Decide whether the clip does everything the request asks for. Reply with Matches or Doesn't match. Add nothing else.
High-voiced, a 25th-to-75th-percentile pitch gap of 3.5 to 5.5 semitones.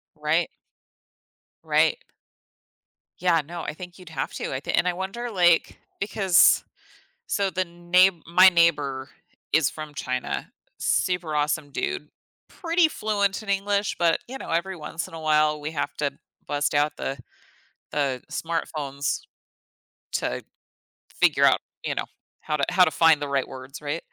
Doesn't match